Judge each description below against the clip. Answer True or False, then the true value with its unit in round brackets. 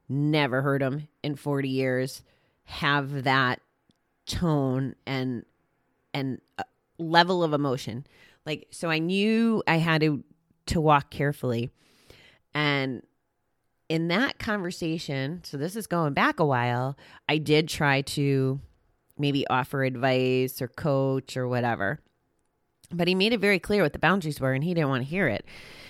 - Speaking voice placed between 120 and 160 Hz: True (140 Hz)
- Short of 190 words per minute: True (145 wpm)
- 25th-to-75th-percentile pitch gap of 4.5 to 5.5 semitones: False (3.8 semitones)